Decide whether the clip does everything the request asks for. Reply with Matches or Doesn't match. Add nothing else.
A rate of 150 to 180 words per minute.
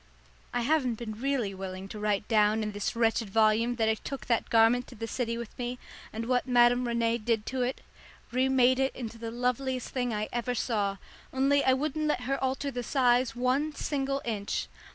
Doesn't match